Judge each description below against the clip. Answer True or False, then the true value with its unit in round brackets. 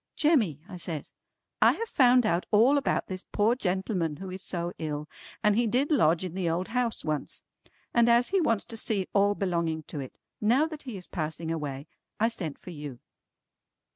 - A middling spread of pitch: False (6.3 semitones)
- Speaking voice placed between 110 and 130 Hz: False (190 Hz)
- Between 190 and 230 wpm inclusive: True (195 wpm)